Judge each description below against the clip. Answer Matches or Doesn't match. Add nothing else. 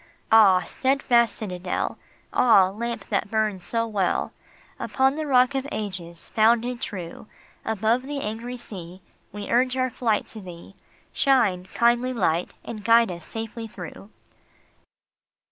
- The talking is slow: Matches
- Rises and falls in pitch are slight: Doesn't match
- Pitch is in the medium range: Doesn't match